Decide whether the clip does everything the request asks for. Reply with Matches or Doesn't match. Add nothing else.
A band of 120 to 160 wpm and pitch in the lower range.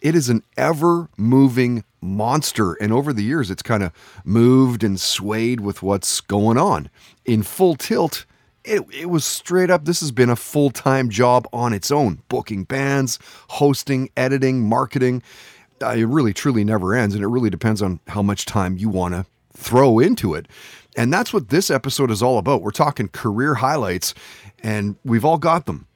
Doesn't match